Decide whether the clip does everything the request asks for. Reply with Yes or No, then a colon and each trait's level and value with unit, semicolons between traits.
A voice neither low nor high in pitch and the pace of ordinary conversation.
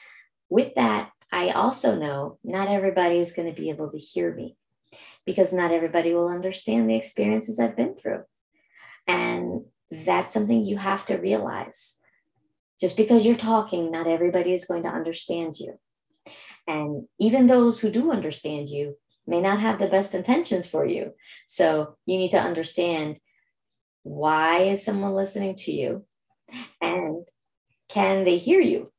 Yes: medium, 175 Hz; average, 155 wpm